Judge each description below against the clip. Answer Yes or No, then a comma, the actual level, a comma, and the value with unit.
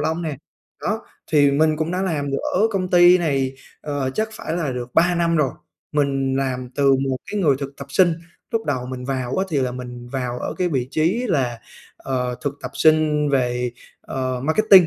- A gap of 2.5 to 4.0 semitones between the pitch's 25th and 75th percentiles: No, average, 4.6 semitones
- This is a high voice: No, medium, 145 Hz